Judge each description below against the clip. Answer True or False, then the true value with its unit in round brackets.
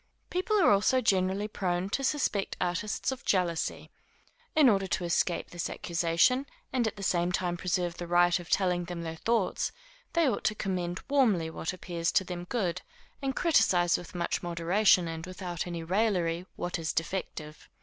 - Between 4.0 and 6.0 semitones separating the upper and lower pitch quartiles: False (3.4 semitones)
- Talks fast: False (170 wpm)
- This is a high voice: False (180 Hz)